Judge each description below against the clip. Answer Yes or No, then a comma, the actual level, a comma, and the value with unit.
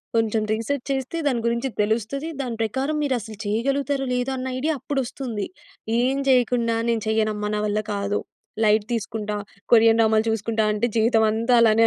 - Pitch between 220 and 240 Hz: Yes, high, 230 Hz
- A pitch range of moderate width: Yes, average, 3.2 semitones